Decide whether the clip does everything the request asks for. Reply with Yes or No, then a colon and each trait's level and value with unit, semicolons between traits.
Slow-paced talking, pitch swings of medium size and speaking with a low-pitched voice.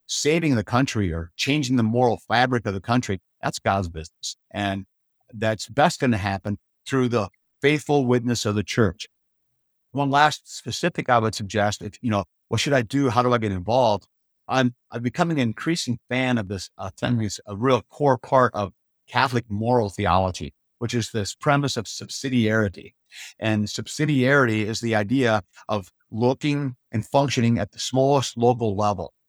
No: average, 170 wpm; average, 4.1 semitones; low, 120 Hz